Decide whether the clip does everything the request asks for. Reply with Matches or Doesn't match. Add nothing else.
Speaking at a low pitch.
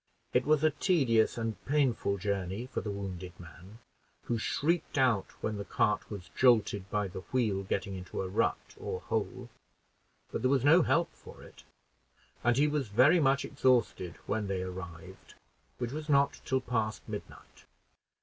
Matches